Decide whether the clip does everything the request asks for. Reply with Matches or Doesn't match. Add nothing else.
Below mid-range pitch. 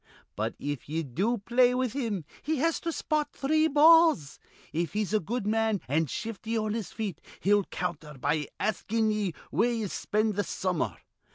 Doesn't match